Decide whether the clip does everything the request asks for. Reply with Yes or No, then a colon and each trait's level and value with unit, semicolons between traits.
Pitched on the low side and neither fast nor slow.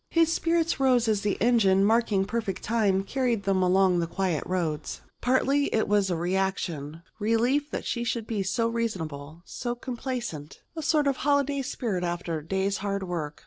No: high, 205 Hz; average, 175 wpm